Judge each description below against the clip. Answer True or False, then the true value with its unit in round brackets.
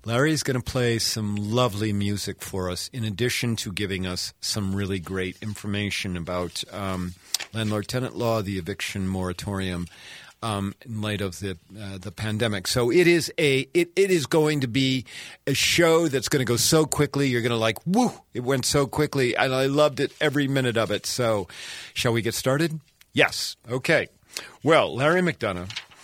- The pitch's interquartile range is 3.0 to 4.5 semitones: False (5.4 semitones)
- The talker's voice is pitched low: True (115 Hz)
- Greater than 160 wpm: True (180 wpm)